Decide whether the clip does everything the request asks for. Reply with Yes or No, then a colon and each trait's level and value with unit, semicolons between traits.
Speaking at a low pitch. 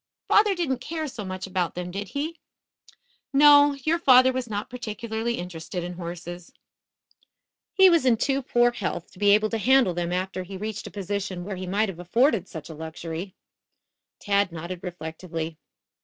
No: high, 200 Hz